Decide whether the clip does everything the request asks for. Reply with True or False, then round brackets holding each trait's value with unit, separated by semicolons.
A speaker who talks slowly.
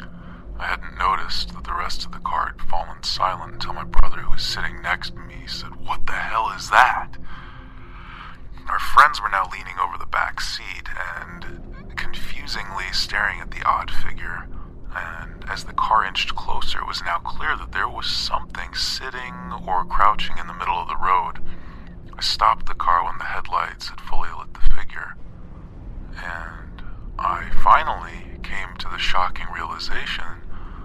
False (165 wpm)